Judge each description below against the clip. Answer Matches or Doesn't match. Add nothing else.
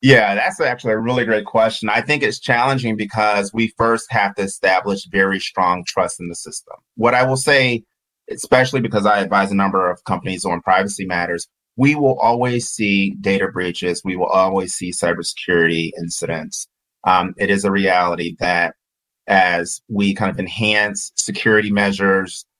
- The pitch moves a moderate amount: Matches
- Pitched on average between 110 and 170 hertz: Doesn't match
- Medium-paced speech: Matches